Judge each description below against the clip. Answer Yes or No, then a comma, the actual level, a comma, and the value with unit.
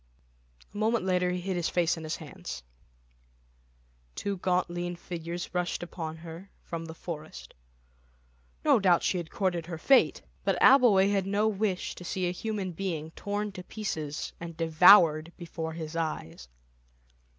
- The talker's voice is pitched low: No, medium, 175 Hz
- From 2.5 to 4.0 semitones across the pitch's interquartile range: Yes, average, 3.0 semitones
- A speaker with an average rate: Yes, average, 155 wpm